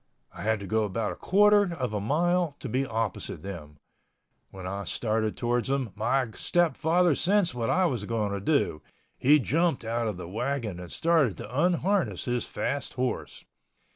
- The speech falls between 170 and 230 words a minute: Yes, average, 175 wpm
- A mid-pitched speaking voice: No, low, 125 Hz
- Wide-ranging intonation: Yes, wide, 7.4 semitones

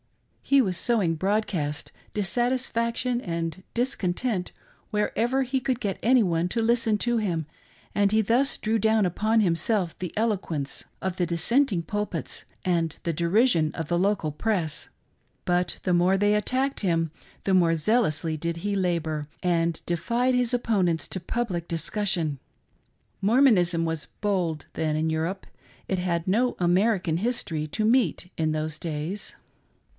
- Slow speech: No, average, 150 wpm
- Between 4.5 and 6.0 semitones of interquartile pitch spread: Yes, average, 5.1 semitones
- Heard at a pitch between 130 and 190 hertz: Yes, medium, 185 Hz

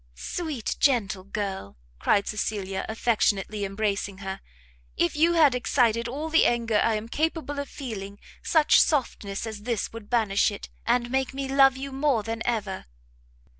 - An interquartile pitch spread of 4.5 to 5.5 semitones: Yes, average, 4.9 semitones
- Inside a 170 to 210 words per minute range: No, average, 155 wpm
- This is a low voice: No, high, 230 Hz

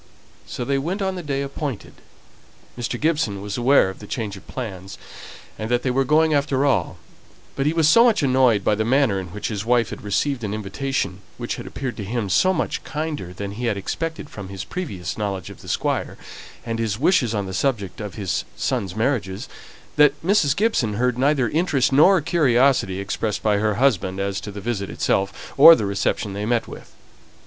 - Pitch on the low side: Yes, low, 120 Hz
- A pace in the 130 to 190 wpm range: No, average, 200 wpm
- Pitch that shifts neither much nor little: No, wide, 5.8 semitones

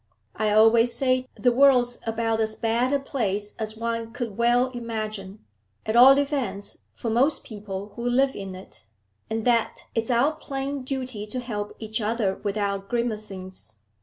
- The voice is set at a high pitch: Yes, high, 230 Hz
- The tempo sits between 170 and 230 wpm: No, average, 160 wpm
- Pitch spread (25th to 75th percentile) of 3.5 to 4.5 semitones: No, average, 2.9 semitones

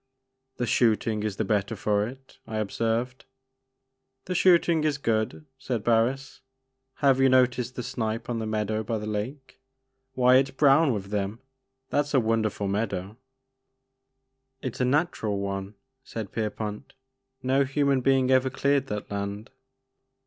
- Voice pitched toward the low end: Yes, low, 115 Hz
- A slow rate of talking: No, average, 155 wpm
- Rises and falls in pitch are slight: No, average, 3.8 semitones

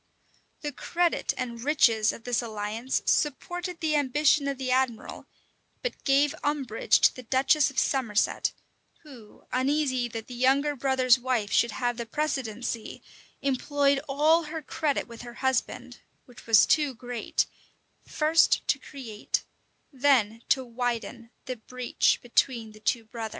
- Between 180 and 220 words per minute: No, average, 140 wpm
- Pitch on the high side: Yes, very high, 255 Hz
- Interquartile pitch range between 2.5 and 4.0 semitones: Yes, average, 3.5 semitones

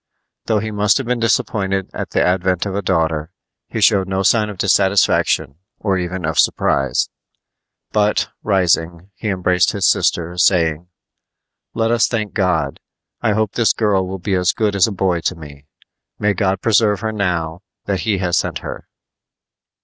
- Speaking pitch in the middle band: No, very low, 95 Hz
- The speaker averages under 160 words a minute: No, average, 170 wpm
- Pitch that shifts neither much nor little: Yes, average, 3.0 semitones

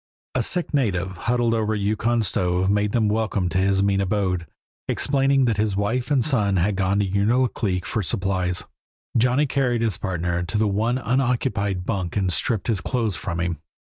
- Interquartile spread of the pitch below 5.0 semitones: Yes, average, 3.9 semitones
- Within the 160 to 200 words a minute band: Yes, average, 180 wpm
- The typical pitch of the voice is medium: No, low, 105 Hz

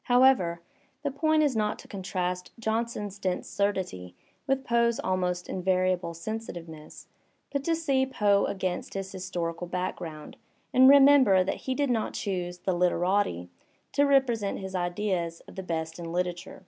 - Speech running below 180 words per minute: Yes, average, 150 wpm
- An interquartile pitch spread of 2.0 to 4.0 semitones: No, average, 5.0 semitones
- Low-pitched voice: No, high, 190 Hz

